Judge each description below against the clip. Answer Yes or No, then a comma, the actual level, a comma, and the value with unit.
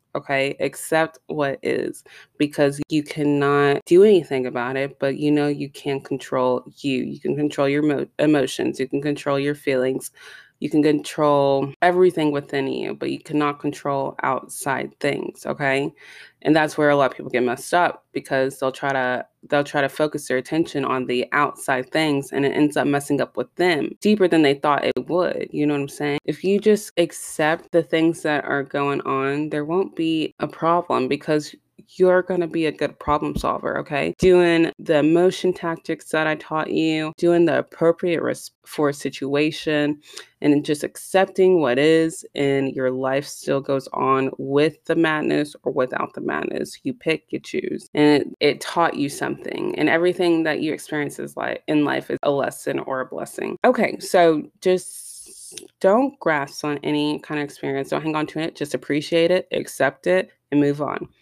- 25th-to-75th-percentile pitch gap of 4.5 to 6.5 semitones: No, average, 3.0 semitones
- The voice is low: No, medium, 150 Hz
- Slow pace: No, average, 185 wpm